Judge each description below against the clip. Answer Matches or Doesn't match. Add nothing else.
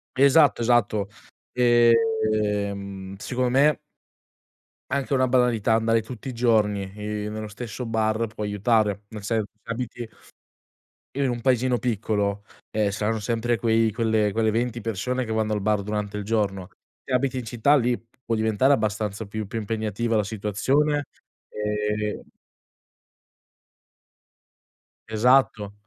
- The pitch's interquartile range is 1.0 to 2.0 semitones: Doesn't match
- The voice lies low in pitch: Matches